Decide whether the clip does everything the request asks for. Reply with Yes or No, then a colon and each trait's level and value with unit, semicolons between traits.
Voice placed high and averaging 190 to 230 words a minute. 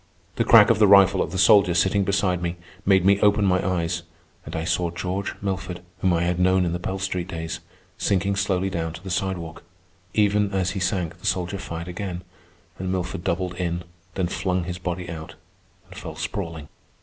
No: very low, 90 Hz; average, 195 wpm